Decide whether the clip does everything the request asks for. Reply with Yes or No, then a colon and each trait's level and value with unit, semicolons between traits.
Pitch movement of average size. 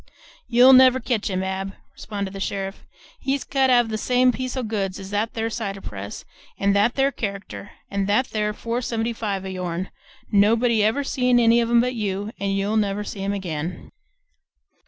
Yes: average, 3.5 semitones